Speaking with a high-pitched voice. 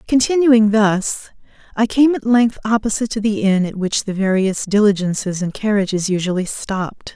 Yes: high, 210 Hz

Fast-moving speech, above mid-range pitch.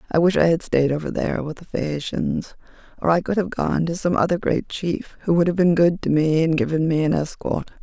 No: fast, 245 wpm; medium, 165 Hz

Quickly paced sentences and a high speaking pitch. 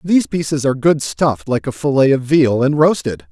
No: fast, 215 wpm; medium, 140 Hz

